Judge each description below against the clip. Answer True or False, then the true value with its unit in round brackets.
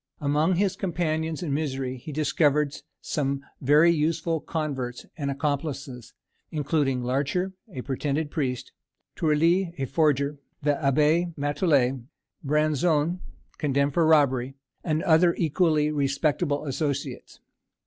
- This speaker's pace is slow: True (110 wpm)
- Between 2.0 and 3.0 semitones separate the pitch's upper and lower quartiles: True (2.6 semitones)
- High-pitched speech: False (150 Hz)